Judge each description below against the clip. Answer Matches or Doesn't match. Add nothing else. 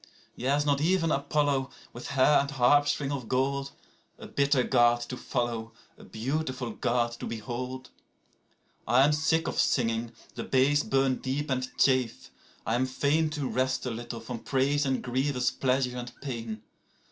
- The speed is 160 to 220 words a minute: Doesn't match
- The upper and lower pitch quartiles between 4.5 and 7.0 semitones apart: Doesn't match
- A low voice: Matches